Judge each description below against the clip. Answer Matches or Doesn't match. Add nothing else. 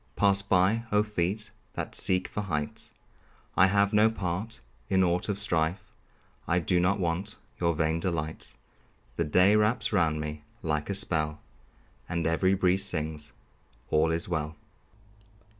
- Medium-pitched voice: Doesn't match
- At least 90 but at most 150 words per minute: Matches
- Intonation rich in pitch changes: Doesn't match